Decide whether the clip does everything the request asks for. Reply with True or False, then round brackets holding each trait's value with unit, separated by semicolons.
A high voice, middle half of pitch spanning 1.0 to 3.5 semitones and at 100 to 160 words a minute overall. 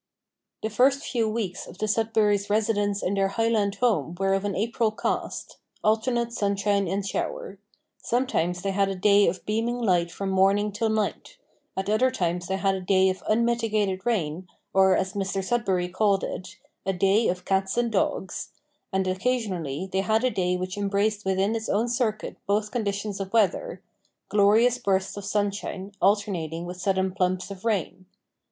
False (200 Hz; 2.4 semitones; 170 wpm)